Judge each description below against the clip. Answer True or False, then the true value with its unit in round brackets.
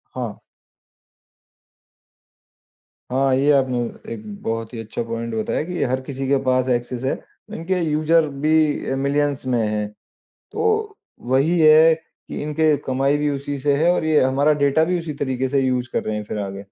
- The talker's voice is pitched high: False (135 Hz)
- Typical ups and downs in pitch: True (3.5 semitones)